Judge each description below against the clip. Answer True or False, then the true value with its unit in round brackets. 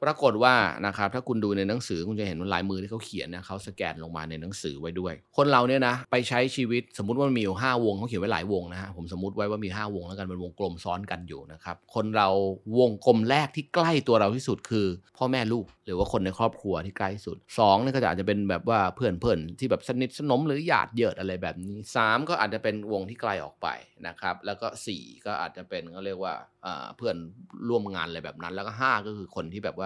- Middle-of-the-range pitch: False (100 Hz)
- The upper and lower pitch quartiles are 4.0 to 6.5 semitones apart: True (4.6 semitones)